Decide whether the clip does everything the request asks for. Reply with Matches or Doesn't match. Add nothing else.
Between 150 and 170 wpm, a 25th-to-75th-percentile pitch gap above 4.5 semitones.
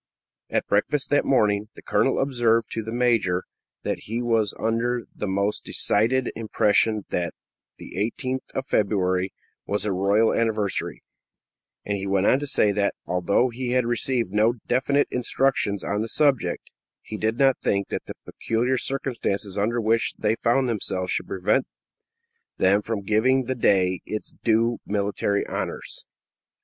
Doesn't match